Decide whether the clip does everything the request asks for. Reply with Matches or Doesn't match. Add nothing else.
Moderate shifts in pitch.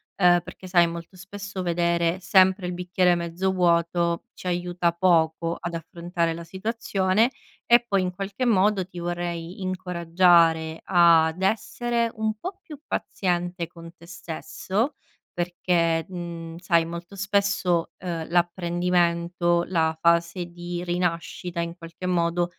Doesn't match